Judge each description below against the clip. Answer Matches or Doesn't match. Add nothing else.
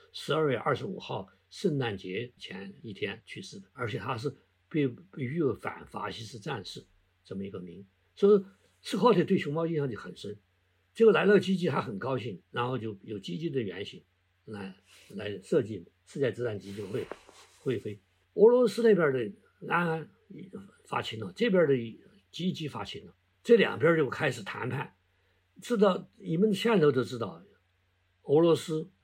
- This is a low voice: Matches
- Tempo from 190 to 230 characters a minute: Doesn't match